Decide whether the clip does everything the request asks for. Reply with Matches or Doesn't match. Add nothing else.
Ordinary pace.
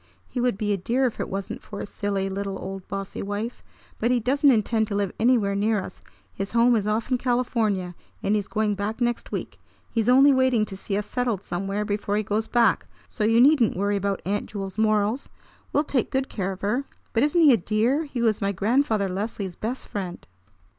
Doesn't match